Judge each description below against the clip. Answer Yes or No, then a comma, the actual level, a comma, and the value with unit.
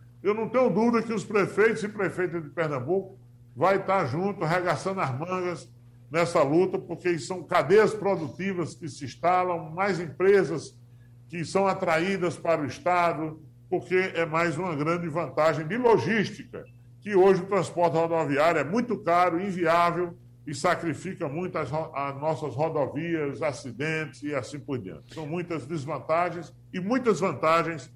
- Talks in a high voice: No, medium, 170 Hz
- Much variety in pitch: No, average, 3.7 semitones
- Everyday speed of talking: Yes, average, 150 wpm